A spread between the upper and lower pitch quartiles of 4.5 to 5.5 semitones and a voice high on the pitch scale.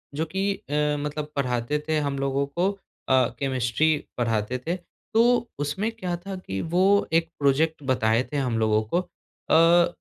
No: average, 5.2 semitones; medium, 150 Hz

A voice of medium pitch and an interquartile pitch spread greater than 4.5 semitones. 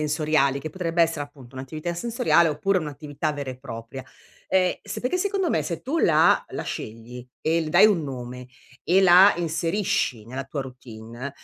Yes: medium, 155 Hz; average, 4.9 semitones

